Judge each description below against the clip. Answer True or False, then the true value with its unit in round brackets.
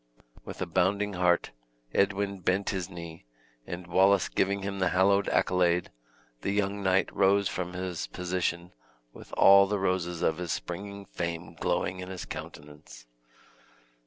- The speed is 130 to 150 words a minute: True (145 wpm)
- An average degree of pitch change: False (2.1 semitones)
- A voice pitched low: True (95 Hz)